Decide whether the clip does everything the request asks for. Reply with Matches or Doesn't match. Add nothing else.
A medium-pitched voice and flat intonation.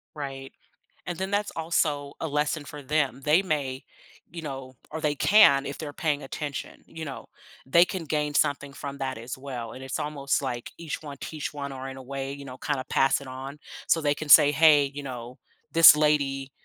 Matches